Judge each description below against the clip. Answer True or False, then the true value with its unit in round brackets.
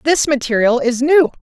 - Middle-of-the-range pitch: False (270 Hz)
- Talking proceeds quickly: False (170 wpm)